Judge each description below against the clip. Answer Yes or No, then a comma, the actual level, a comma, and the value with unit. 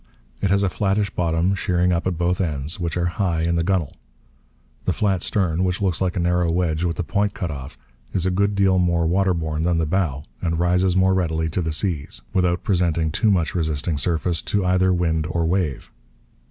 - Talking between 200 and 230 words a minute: Yes, fast, 205 wpm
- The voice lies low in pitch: Yes, very low, 90 Hz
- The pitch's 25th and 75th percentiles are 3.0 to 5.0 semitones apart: No, narrow, 2.4 semitones